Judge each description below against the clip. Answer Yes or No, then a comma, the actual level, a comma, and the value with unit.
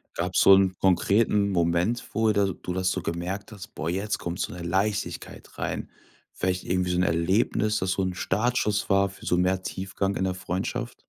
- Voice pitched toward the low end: Yes, very low, 95 Hz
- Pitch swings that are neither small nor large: No, narrow, 2.2 semitones